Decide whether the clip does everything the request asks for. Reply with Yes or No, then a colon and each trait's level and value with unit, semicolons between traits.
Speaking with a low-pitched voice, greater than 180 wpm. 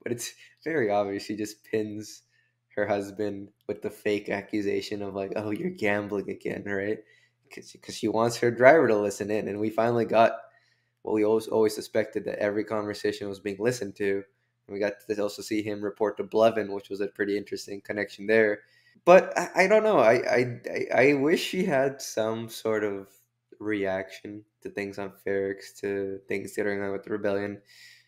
Yes: low, 105 Hz; average, 190 wpm